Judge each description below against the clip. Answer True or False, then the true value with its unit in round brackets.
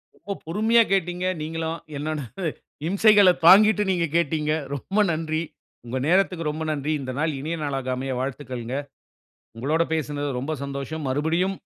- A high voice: False (155 Hz)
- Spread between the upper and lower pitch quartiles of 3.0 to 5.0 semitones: True (4.2 semitones)